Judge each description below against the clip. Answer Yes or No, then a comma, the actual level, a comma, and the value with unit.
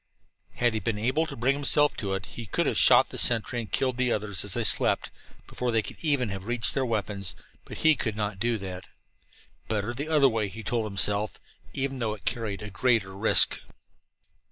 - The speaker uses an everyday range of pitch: Yes, average, 3.4 semitones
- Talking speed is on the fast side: Yes, fast, 210 wpm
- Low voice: Yes, low, 115 Hz